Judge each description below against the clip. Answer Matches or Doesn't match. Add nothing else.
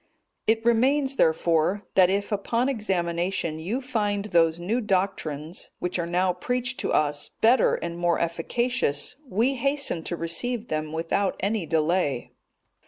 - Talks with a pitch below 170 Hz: Doesn't match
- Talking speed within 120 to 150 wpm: Matches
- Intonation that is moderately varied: Doesn't match